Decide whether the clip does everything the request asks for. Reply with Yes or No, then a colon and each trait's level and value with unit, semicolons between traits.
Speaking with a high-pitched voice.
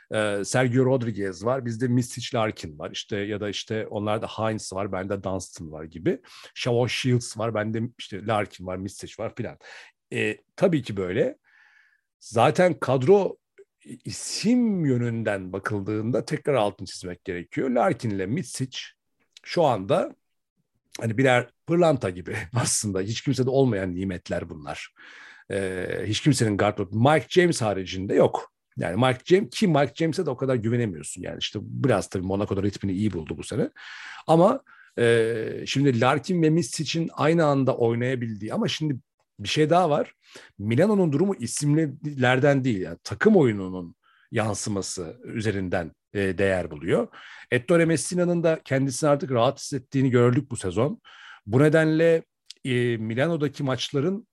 No: low, 120 Hz